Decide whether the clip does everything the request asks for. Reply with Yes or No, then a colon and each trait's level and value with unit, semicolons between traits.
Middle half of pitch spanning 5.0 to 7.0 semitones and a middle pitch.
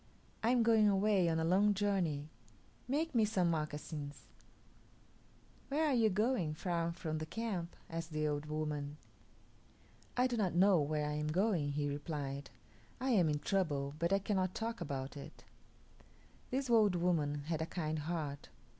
Yes: wide, 5.5 semitones; medium, 170 Hz